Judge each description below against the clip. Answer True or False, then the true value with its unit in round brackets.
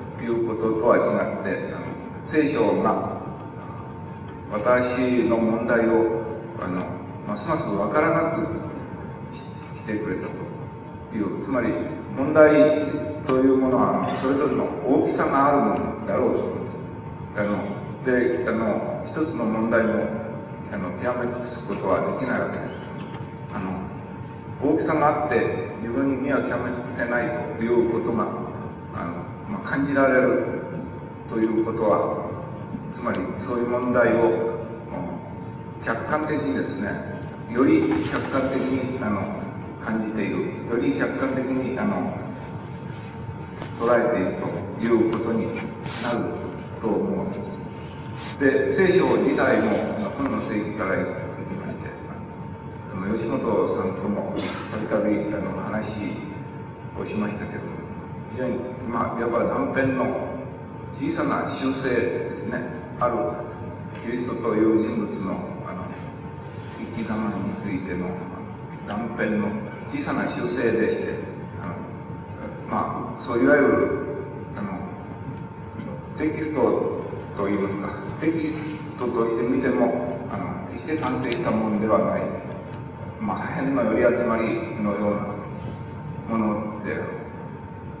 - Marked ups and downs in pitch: False (3.5 semitones)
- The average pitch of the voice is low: True (115 Hz)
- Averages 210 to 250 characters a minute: True (235 characters per minute)